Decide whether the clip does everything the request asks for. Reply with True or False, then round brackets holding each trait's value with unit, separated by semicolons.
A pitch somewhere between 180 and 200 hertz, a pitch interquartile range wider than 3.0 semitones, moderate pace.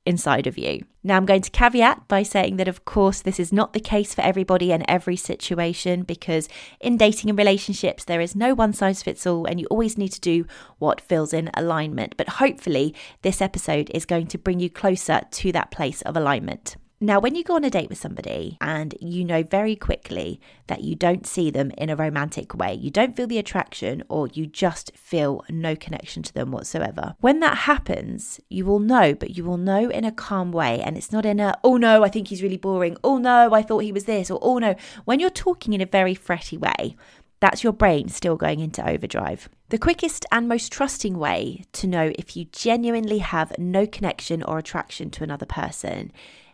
False (190 Hz; 4.1 semitones; 215 wpm)